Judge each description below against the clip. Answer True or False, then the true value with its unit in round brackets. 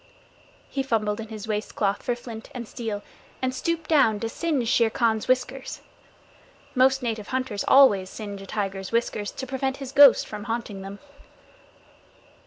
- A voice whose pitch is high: True (230 Hz)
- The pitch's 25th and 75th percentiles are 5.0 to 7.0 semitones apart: False (3.8 semitones)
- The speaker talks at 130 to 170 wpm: True (160 wpm)